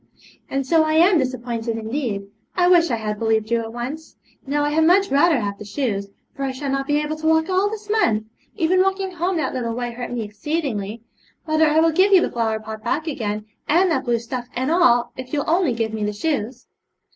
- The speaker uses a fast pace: Yes, fast, 225 wpm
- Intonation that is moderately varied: No, wide, 6.0 semitones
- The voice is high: Yes, very high, 270 Hz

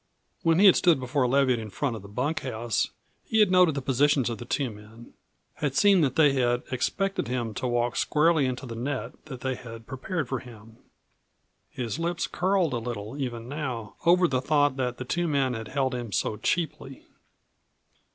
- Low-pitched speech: Yes, low, 130 Hz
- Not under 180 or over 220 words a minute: Yes, average, 190 wpm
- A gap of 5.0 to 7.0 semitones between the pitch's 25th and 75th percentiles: No, average, 4.1 semitones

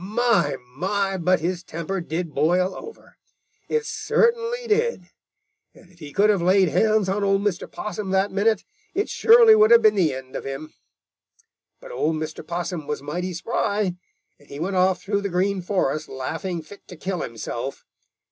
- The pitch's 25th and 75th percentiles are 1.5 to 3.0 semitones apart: No, average, 4.0 semitones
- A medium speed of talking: Yes, average, 175 wpm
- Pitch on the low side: No, high, 190 Hz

